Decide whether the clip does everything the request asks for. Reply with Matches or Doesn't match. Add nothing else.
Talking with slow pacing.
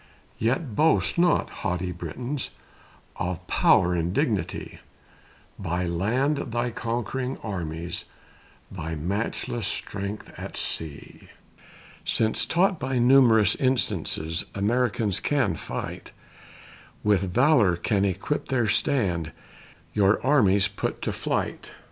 Matches